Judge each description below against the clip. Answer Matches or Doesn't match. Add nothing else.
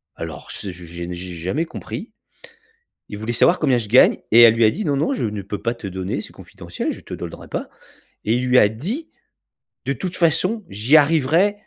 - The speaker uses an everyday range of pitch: Doesn't match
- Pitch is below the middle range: Matches